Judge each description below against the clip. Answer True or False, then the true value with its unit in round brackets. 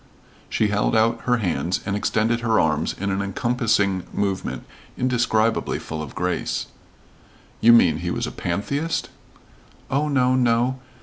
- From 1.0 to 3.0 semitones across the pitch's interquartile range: False (3.9 semitones)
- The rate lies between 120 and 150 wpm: True (140 wpm)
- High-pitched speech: False (110 Hz)